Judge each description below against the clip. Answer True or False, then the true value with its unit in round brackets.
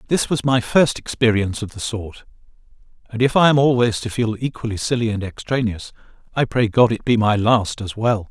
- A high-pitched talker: False (115 Hz)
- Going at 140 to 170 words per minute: False (200 wpm)